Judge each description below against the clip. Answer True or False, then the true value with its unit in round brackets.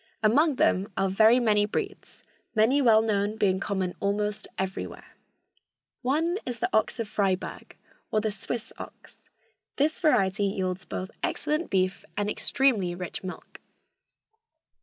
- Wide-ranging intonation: False (4.2 semitones)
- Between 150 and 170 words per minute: False (135 wpm)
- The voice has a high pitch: True (210 Hz)